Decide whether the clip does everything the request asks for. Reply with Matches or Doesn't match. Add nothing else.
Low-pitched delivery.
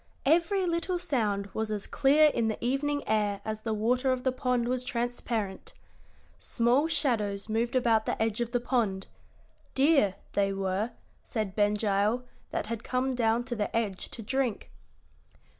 Doesn't match